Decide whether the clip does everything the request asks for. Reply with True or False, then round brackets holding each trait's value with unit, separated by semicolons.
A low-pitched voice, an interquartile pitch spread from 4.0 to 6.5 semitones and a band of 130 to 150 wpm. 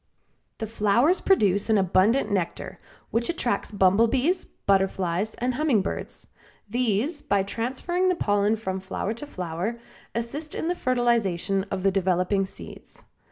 False (215 Hz; 4.6 semitones; 135 wpm)